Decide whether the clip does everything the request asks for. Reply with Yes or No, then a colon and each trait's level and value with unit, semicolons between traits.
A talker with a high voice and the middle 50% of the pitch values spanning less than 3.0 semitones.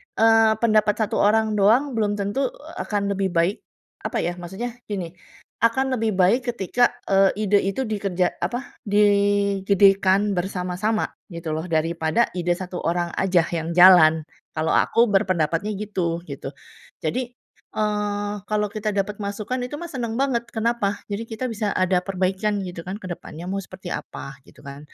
No: high, 200 Hz; average, 3.3 semitones